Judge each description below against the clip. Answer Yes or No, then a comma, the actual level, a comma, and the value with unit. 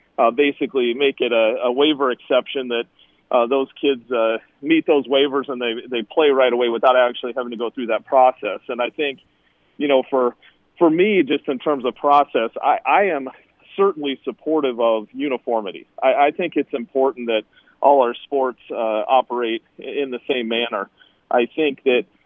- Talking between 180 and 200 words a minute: Yes, average, 185 wpm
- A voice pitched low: Yes, low, 130 Hz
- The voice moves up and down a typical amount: Yes, average, 3.3 semitones